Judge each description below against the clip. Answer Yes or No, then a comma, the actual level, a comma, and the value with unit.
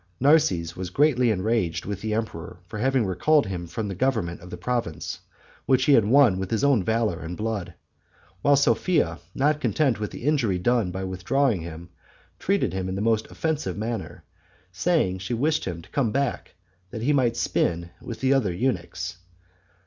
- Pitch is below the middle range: Yes, low, 110 Hz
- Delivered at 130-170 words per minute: No, average, 180 wpm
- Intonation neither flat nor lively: No, wide, 6.5 semitones